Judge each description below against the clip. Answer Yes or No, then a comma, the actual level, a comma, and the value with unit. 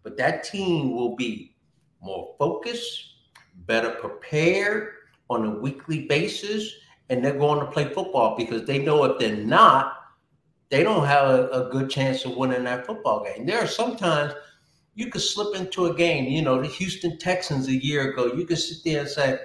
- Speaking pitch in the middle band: Yes, medium, 145 Hz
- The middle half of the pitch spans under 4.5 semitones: No, wide, 5.6 semitones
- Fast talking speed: No, average, 185 wpm